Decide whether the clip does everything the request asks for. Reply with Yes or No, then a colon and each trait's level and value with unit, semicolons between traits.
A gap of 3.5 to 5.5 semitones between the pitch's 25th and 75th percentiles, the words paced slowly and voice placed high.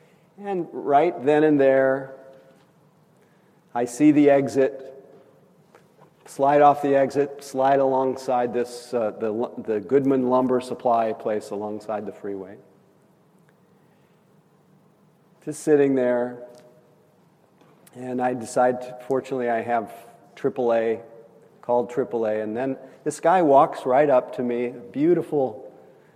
No: average, 3.8 semitones; slow, 110 wpm; low, 135 Hz